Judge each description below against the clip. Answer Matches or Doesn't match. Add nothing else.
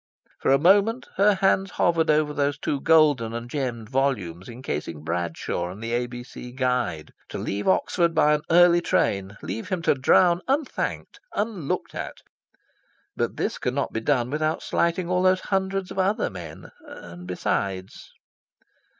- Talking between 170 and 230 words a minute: Doesn't match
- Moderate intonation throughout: Doesn't match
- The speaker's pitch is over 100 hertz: Matches